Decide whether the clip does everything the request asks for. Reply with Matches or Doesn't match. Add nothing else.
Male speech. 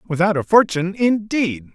Matches